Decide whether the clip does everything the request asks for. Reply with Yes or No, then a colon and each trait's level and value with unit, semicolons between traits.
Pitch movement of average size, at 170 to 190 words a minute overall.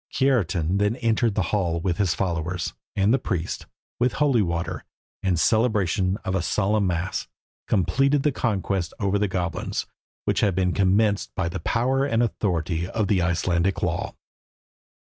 No: average, 3.9 semitones; average, 155 wpm